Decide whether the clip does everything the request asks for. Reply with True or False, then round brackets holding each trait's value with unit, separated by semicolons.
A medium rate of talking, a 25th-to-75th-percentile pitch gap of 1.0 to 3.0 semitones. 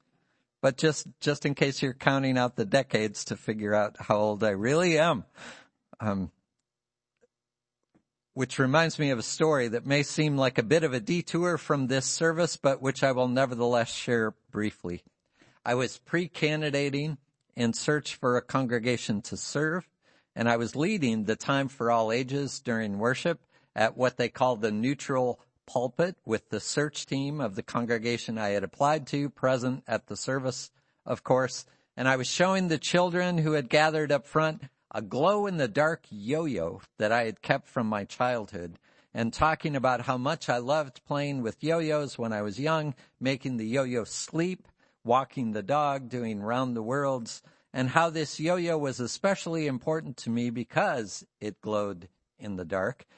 False (175 wpm; 4.4 semitones)